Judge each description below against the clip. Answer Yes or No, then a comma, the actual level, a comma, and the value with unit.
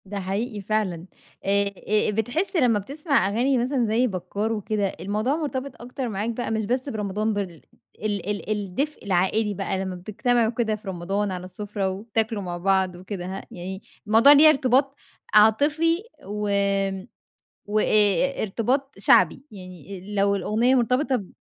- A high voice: Yes, high, 210 Hz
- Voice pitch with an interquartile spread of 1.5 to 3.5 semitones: No, average, 4.0 semitones